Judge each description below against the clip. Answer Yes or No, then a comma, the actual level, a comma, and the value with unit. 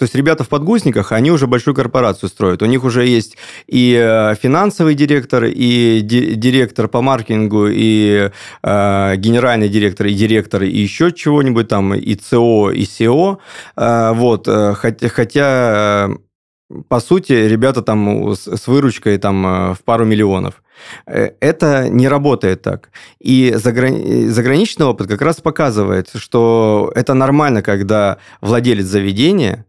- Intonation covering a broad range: No, average, 4.0 semitones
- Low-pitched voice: Yes, low, 115 Hz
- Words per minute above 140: No, average, 130 wpm